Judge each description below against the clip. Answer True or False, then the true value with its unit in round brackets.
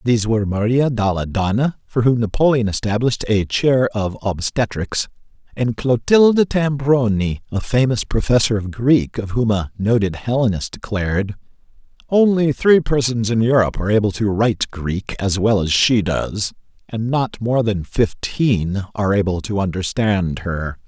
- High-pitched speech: False (110 Hz)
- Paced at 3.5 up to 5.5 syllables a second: True (4.7 syllables/s)